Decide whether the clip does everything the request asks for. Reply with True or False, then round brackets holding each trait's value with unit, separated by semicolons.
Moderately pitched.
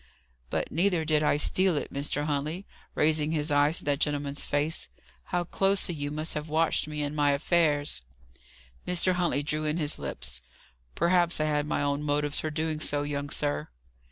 True (150 Hz)